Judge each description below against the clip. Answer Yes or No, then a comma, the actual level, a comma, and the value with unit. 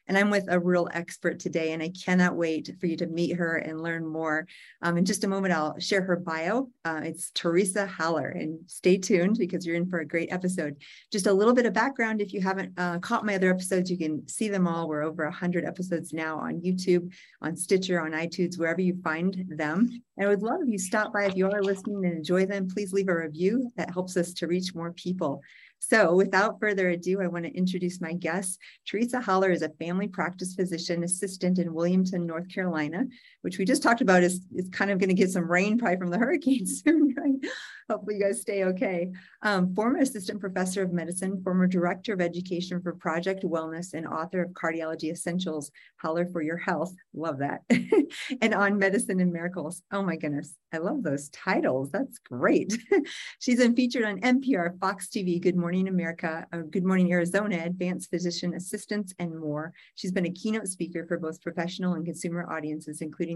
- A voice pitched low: No, medium, 180 Hz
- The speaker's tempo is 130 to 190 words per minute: No, fast, 205 wpm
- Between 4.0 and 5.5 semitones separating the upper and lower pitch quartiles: No, average, 2.9 semitones